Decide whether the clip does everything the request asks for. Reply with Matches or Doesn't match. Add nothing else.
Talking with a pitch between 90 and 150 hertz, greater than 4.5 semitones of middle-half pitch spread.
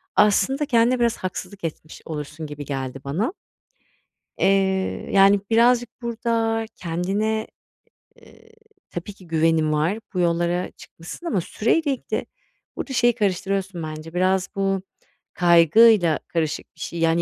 Doesn't match